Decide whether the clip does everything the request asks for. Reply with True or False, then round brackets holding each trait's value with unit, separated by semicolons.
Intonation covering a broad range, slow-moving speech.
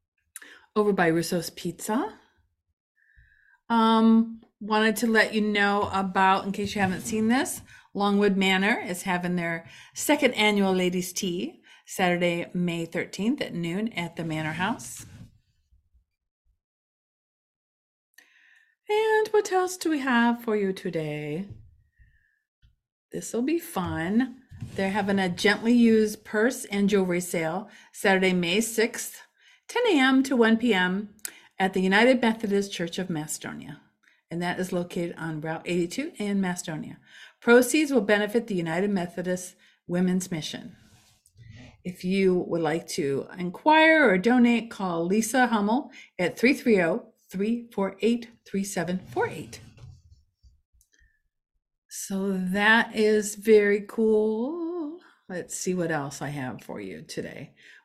False (5.0 semitones; 120 wpm)